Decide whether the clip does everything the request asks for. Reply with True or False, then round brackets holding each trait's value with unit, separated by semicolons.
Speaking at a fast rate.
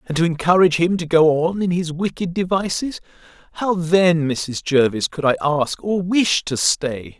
False (175 wpm)